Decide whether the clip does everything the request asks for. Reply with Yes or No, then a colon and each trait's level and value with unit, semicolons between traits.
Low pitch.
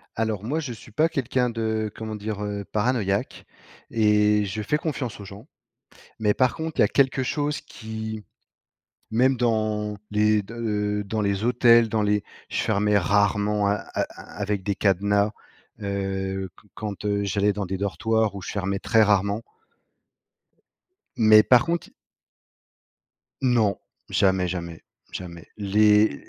Yes: low, 105 Hz